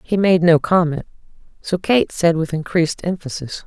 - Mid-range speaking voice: Yes, medium, 170 Hz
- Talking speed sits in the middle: Yes, average, 165 wpm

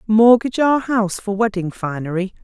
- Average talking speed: Yes, average, 150 wpm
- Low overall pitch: No, high, 210 Hz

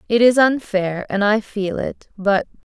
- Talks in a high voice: Yes, high, 210 Hz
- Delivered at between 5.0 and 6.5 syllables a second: No, 4.1 syllables/s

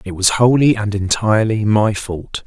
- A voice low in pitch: Yes, low, 105 Hz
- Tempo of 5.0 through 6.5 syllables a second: No, 4.6 syllables/s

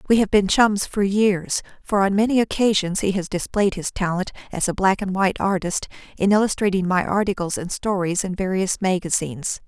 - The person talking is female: Yes, female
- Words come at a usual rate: Yes, average, 185 wpm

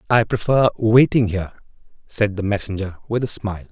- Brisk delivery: No, average, 160 wpm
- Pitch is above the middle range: No, low, 105 Hz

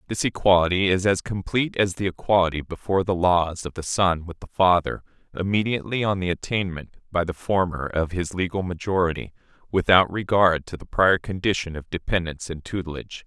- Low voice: Yes, very low, 90 Hz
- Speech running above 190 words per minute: No, average, 170 wpm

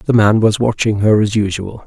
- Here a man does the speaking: Yes, male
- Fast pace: Yes, fast, 225 wpm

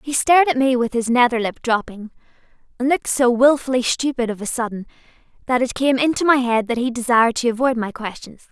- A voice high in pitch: Yes, high, 245 Hz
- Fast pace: Yes, fast, 210 wpm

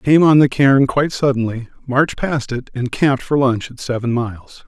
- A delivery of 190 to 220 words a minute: Yes, fast, 205 wpm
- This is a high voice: No, low, 130 Hz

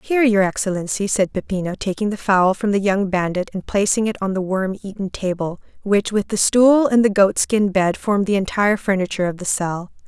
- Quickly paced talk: Yes, fast, 215 wpm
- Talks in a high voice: Yes, high, 200 Hz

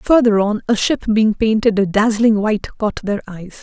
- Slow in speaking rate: No, average, 200 wpm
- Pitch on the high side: Yes, high, 215 Hz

